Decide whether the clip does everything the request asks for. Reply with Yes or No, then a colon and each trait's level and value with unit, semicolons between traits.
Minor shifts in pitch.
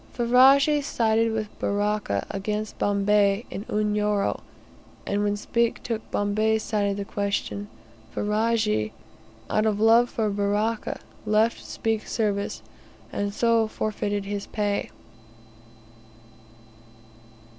Yes: narrow, 1.6 semitones